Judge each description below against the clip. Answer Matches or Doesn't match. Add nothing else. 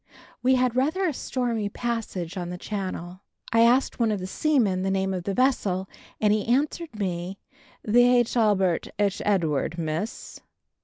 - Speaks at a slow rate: Doesn't match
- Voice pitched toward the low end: Doesn't match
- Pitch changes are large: Doesn't match